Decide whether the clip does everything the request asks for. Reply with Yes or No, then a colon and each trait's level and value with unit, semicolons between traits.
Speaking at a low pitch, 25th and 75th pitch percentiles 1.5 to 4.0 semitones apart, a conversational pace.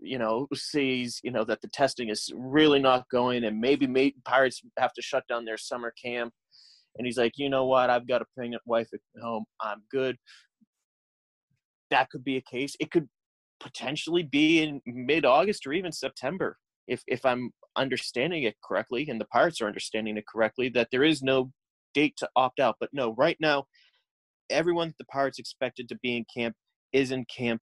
Yes: low, 130 Hz; average, 2.8 semitones; average, 195 wpm